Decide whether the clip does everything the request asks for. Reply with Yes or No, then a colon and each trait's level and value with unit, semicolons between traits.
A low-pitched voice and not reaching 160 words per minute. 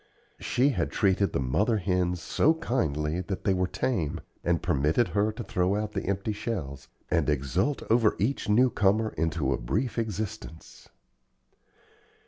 Yes: very low, 95 Hz; average, 150 wpm